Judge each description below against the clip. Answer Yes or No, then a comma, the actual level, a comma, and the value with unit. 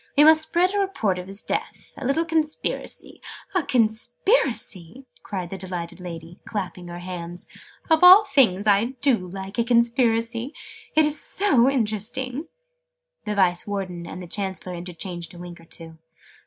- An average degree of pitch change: No, wide, 7.2 semitones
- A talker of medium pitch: No, high, 210 Hz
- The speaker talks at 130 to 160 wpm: Yes, average, 155 wpm